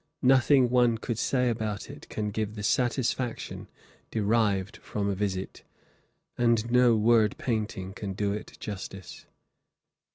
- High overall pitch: No, low, 110 Hz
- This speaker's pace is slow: Yes, slow, 130 wpm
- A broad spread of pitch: No, average, 2.8 semitones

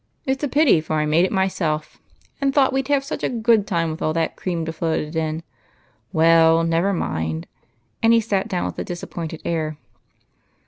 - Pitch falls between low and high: Yes, medium, 170 Hz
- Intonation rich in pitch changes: Yes, wide, 6.0 semitones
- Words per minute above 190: Yes, average, 200 wpm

